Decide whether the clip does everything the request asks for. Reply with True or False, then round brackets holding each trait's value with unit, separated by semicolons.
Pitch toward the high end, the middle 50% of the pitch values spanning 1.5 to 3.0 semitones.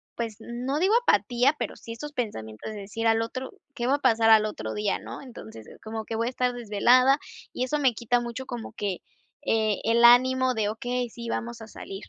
True (235 Hz; 2.5 semitones)